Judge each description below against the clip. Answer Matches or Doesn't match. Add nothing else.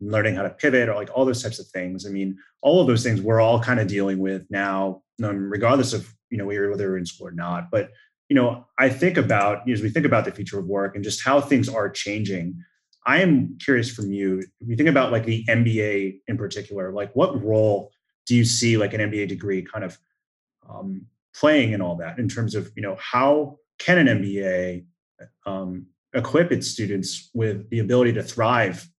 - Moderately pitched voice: Doesn't match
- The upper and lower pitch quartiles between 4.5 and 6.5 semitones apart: Doesn't match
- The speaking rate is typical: Doesn't match